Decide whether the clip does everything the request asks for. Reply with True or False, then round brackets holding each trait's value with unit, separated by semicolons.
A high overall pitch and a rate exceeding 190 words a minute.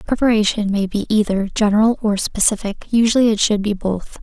False (210 Hz; 170 wpm)